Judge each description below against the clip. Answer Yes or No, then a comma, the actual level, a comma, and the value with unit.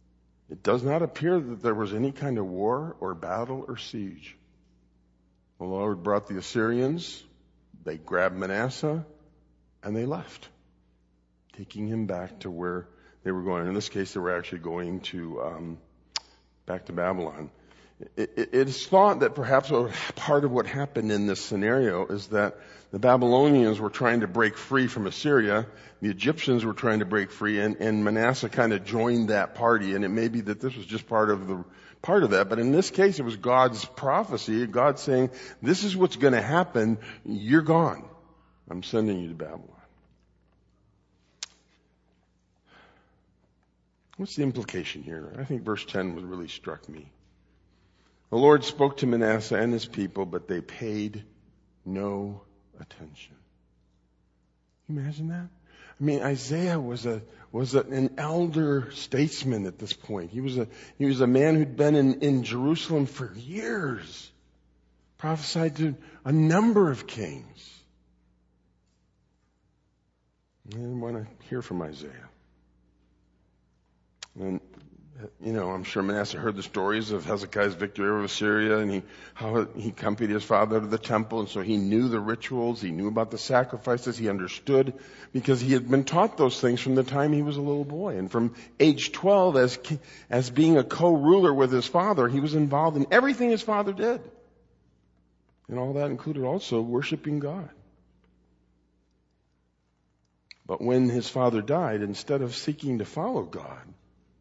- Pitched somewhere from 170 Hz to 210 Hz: No, low, 110 Hz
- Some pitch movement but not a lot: No, wide, 6.9 semitones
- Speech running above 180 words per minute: No, average, 160 wpm